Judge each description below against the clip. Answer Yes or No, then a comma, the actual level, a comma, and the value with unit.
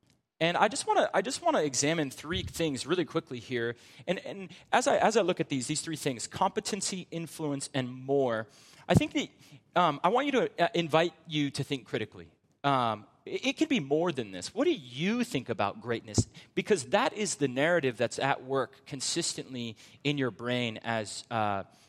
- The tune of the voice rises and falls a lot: Yes, wide, 6.2 semitones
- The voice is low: No, medium, 145 Hz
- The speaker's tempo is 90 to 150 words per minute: No, average, 195 wpm